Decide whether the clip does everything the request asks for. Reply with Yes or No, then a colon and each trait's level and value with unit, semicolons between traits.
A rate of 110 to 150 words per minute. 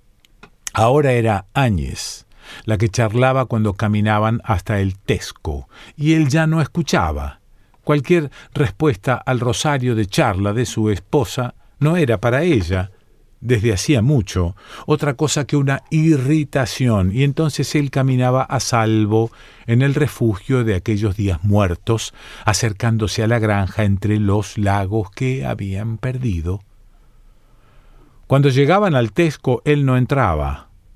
Yes: average, 130 wpm